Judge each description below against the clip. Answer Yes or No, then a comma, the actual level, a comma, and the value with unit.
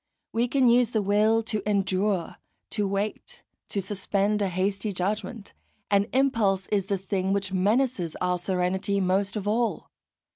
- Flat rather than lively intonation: Yes, narrow, 2.1 semitones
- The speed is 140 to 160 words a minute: Yes, average, 150 wpm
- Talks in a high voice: Yes, high, 200 Hz